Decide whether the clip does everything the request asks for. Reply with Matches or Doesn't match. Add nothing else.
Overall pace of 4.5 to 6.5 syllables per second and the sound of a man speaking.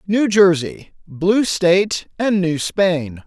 Doesn't match